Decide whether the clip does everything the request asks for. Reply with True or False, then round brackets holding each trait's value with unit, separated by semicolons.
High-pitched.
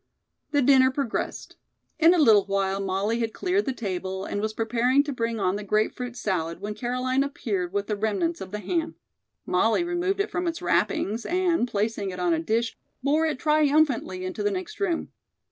True (230 Hz)